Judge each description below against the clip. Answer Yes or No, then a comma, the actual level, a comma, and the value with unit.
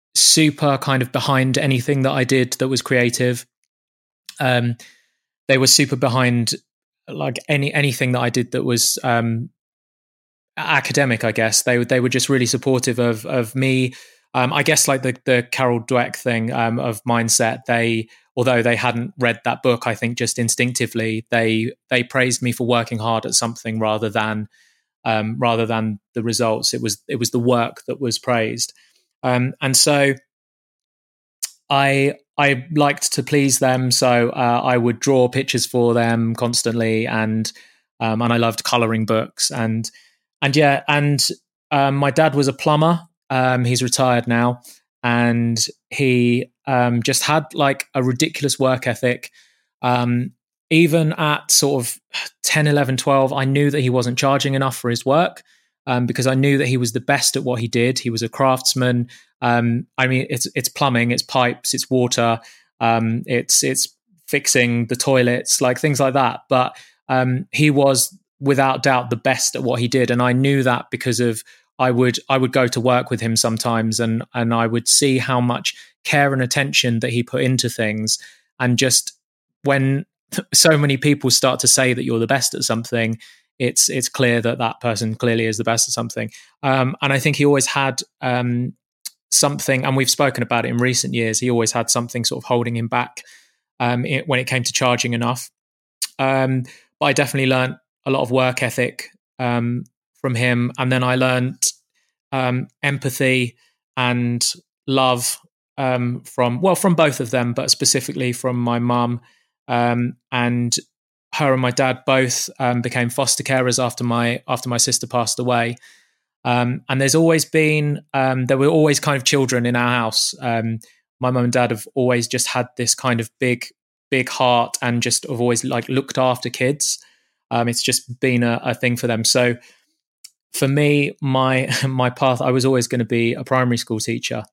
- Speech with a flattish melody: Yes, narrow, 2.1 semitones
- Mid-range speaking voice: No, low, 125 Hz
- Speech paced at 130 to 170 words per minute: No, average, 180 wpm